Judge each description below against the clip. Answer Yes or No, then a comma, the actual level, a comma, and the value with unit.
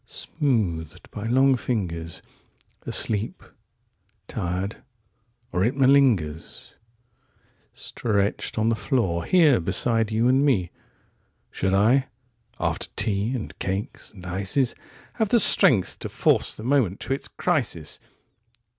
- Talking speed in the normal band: No, slow, 100 wpm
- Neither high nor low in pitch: No, low, 110 Hz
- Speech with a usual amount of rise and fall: No, wide, 5.7 semitones